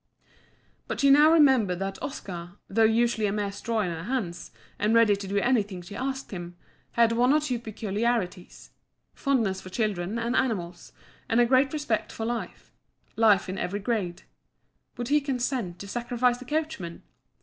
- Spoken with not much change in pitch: No, average, 4.4 semitones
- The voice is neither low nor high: No, high, 225 Hz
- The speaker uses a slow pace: No, average, 170 wpm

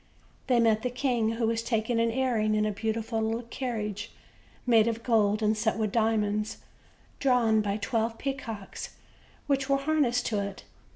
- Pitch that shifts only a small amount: Yes, narrow, 2.3 semitones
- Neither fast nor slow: Yes, average, 165 wpm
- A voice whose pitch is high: Yes, high, 225 Hz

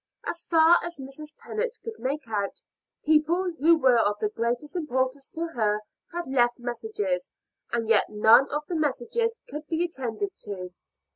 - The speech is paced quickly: No, average, 160 wpm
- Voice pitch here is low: No, very high, 270 Hz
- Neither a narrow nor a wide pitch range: No, wide, 6.4 semitones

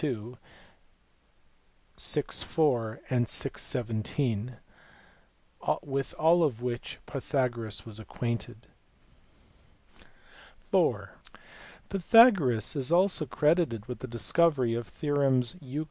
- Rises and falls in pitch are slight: No, average, 4.5 semitones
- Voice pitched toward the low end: Yes, low, 125 Hz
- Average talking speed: No, slow, 95 wpm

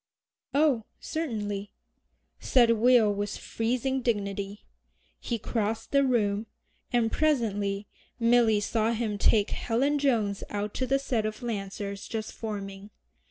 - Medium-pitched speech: No, high, 225 Hz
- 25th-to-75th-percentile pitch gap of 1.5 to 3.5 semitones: Yes, average, 3.0 semitones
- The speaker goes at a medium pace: No, slow, 120 wpm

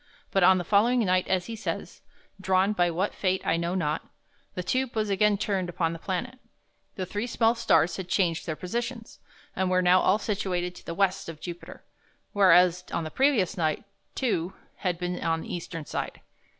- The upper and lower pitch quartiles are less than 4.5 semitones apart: Yes, average, 2.9 semitones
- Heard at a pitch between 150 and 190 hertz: Yes, medium, 185 Hz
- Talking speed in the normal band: Yes, average, 190 wpm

